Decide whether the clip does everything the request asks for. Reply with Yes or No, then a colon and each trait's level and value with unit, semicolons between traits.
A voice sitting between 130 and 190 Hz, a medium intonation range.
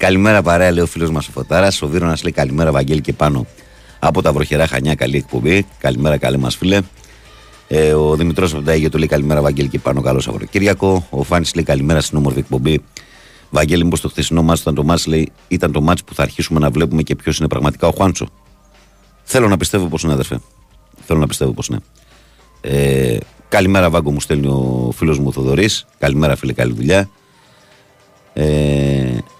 No: very low, 75 Hz; average, 3.5 semitones